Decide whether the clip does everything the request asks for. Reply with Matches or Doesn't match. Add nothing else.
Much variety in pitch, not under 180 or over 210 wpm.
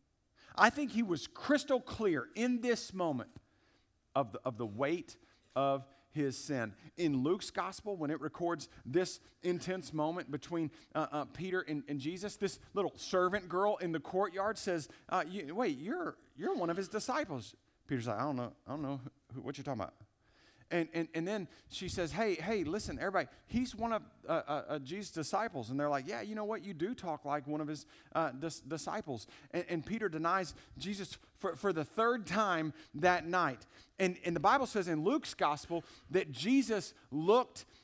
Matches